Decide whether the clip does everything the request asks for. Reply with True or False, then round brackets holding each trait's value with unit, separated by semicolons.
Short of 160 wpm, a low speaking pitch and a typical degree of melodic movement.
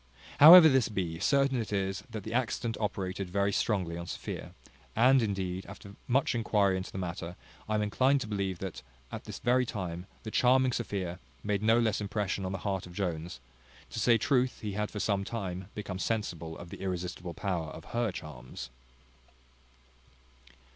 False (175 wpm; 100 Hz; 3.8 semitones)